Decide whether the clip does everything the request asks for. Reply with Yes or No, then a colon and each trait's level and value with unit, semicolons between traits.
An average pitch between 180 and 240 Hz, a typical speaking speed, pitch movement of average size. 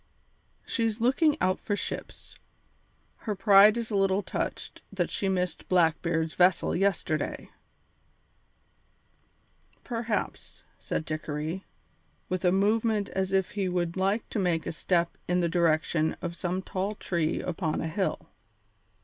No: medium, 185 Hz; slow, 130 wpm; average, 3.1 semitones